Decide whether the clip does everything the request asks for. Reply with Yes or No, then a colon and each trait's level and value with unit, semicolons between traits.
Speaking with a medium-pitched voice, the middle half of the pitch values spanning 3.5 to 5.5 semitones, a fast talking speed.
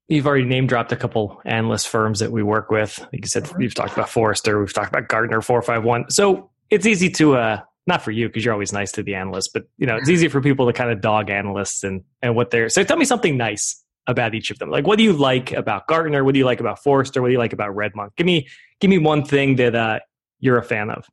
No: low, 120 Hz; average, 4.0 semitones; fast, 275 wpm